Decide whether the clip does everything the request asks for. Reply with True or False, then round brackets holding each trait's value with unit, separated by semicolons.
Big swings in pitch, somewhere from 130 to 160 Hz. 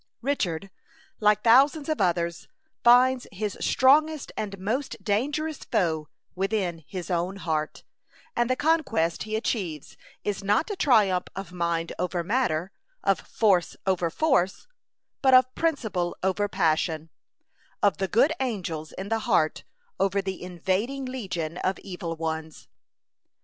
False (6.3 semitones; 195 Hz)